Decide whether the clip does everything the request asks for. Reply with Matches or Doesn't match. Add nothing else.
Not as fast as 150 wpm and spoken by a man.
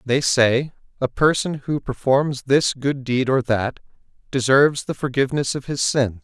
Doesn't match